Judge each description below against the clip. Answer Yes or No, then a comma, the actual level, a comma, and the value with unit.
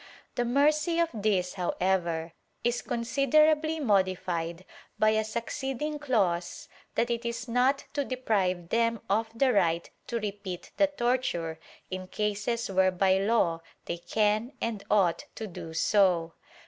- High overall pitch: Yes, high, 215 Hz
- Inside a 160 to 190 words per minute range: No, average, 140 wpm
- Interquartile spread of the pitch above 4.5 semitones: Yes, average, 5.0 semitones